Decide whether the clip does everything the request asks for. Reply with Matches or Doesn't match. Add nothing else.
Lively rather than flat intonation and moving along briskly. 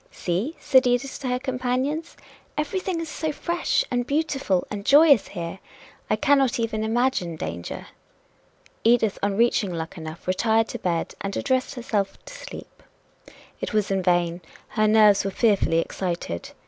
Doesn't match